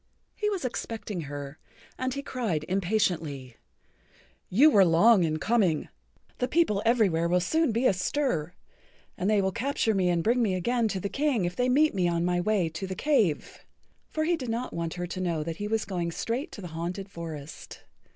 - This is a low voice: No, high, 195 Hz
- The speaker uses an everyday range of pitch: No, wide, 5.9 semitones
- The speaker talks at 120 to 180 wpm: No, average, 195 wpm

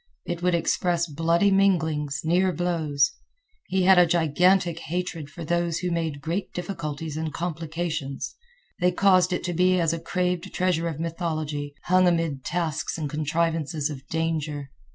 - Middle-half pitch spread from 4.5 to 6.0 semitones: No, narrow, 2.4 semitones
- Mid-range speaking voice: Yes, medium, 165 Hz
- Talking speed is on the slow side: No, average, 155 wpm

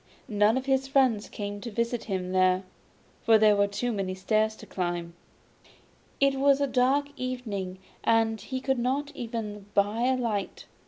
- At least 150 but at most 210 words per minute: Yes, average, 165 wpm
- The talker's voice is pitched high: Yes, high, 225 Hz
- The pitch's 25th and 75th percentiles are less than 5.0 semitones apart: Yes, average, 4.2 semitones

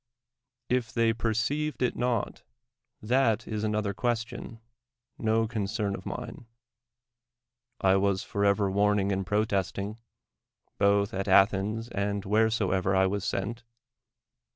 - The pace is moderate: No, slow, 115 wpm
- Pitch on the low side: Yes, low, 105 Hz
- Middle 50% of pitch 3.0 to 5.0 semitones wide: No, narrow, 2.4 semitones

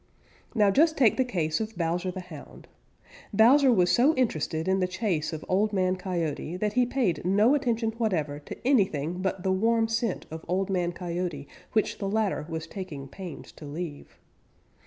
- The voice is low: No, medium, 185 Hz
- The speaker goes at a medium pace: Yes, average, 180 wpm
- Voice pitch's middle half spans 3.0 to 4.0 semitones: No, average, 5.0 semitones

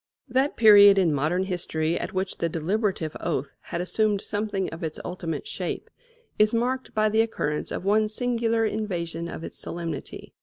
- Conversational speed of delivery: Yes, average, 165 wpm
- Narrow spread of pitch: No, average, 4.5 semitones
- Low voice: No, high, 195 Hz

